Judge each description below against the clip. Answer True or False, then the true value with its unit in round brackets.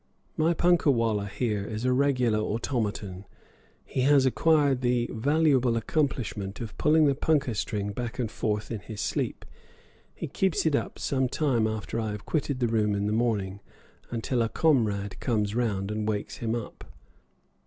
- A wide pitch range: False (4.2 semitones)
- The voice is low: True (115 Hz)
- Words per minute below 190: True (165 wpm)